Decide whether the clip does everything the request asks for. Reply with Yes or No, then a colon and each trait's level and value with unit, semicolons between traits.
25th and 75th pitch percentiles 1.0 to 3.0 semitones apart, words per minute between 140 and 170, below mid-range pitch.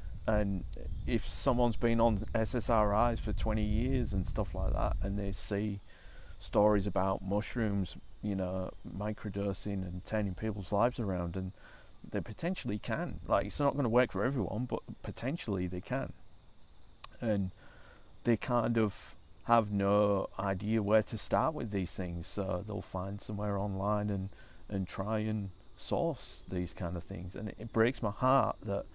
Yes: average, 2.7 semitones; average, 160 wpm; low, 105 Hz